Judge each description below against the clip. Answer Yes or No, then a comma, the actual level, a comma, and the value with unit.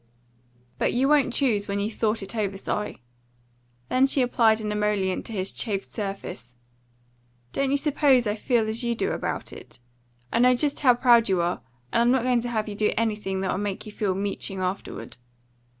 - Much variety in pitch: No, average, 3.5 semitones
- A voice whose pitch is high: Yes, high, 220 Hz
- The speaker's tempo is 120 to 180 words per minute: No, average, 195 wpm